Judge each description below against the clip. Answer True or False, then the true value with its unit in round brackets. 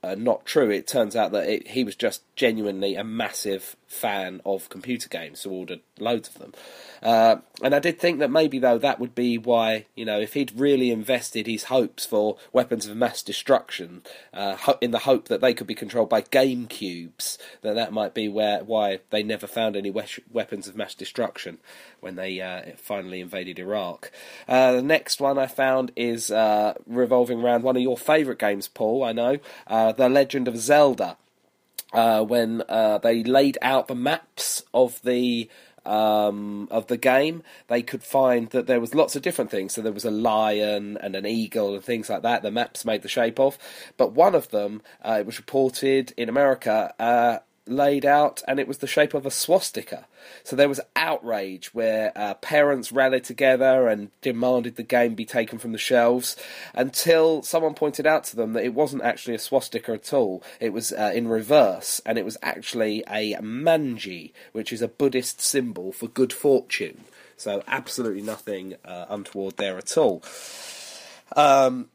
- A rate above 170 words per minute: True (190 wpm)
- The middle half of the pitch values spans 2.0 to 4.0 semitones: True (3.5 semitones)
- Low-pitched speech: True (120 Hz)